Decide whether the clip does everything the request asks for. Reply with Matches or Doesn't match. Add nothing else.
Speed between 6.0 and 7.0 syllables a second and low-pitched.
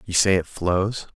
Doesn't match